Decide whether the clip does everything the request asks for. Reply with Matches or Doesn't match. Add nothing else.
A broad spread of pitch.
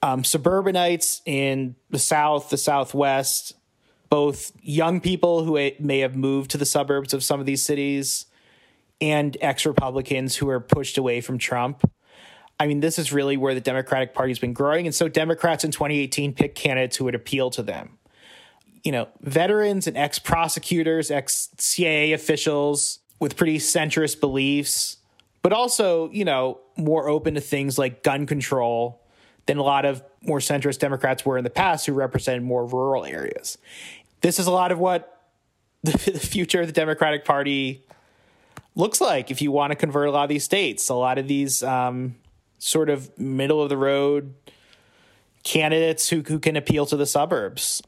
Doesn't match